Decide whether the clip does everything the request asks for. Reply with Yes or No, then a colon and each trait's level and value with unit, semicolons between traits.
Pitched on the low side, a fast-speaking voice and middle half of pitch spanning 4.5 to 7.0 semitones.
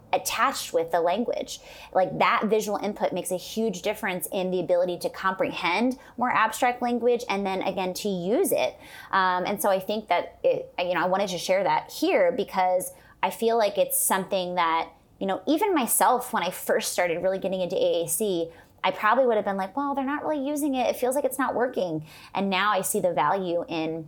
No: high, 195 Hz; fast, 210 wpm; average, 5.1 semitones